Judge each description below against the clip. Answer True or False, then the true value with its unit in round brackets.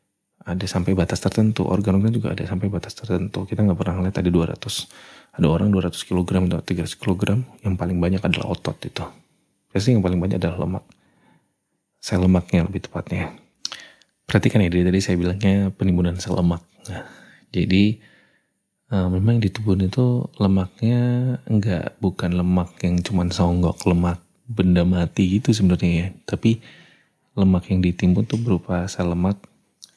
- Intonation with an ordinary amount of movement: False (2.3 semitones)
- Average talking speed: True (150 wpm)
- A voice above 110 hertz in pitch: False (95 Hz)